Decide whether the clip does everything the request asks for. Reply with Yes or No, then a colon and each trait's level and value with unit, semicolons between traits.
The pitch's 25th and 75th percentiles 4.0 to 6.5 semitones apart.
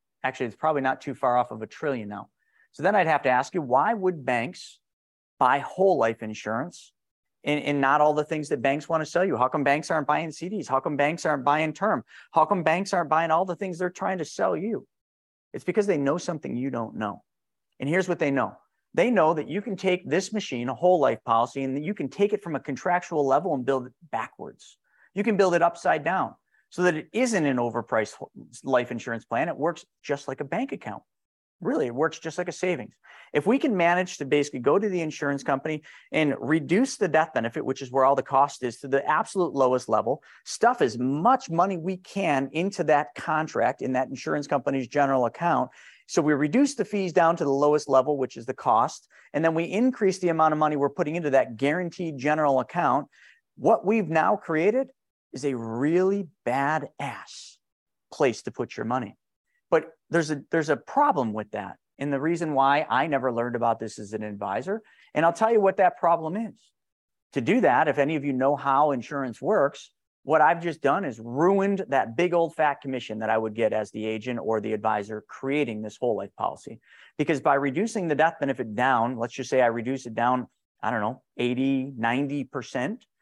Yes: average, 5.1 semitones